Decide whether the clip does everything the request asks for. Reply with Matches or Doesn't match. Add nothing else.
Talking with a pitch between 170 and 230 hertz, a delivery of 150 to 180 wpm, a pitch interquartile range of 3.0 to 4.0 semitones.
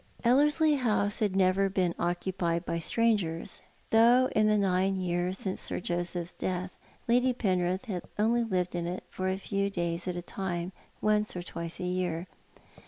Matches